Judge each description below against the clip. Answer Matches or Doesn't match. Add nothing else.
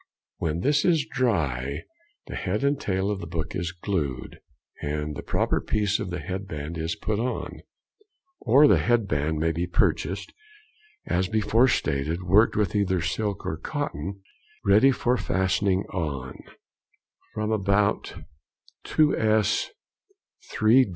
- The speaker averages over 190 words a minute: Doesn't match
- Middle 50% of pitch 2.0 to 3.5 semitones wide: Doesn't match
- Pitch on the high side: Doesn't match